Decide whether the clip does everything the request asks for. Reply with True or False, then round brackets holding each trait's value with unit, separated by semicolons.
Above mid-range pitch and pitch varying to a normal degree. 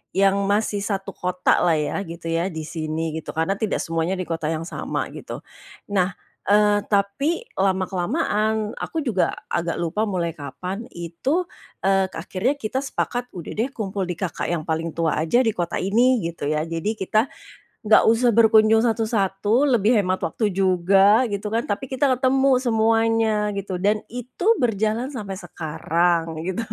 True (200 Hz; 4.5 semitones)